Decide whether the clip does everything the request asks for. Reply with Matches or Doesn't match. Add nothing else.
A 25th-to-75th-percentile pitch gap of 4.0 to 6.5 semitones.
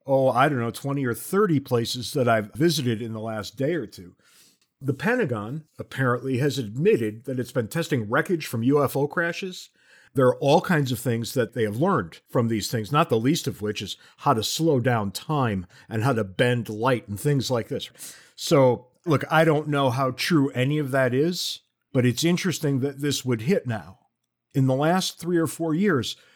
Matches